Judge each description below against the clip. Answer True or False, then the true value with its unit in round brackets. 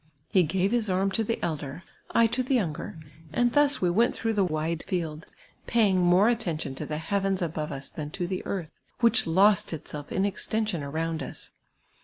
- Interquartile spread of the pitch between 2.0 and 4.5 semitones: False (5.3 semitones)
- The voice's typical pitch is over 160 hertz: True (185 Hz)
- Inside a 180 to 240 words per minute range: True (190 wpm)